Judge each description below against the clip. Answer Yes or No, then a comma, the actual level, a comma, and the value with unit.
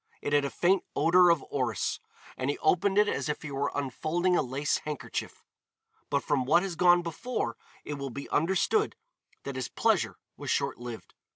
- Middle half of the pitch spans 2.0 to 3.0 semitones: No, average, 4.2 semitones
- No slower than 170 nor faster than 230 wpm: Yes, average, 180 wpm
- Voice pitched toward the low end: No, medium, 150 Hz